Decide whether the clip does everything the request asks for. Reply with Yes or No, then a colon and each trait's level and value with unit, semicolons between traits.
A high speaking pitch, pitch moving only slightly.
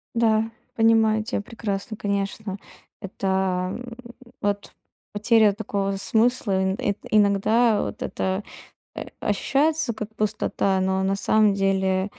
Yes: high, 205 Hz; narrow, 2.2 semitones